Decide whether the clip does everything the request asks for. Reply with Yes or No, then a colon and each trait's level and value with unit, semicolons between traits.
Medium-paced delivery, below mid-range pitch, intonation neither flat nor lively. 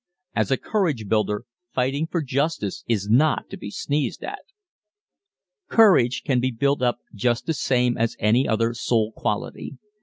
Yes: average, 155 wpm; low, 125 Hz; average, 3.8 semitones